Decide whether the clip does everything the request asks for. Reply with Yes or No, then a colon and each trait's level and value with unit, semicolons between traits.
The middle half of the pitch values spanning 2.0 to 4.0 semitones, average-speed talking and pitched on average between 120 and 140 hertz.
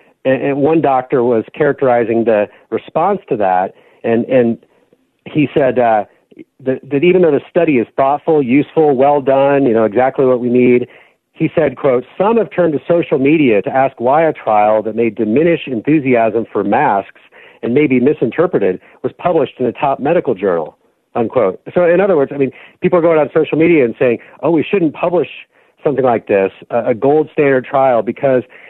No: average, 4.6 semitones; average, 185 wpm; low, 135 Hz